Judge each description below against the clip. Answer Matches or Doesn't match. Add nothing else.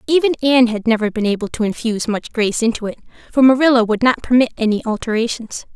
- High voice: Matches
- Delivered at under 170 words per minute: Doesn't match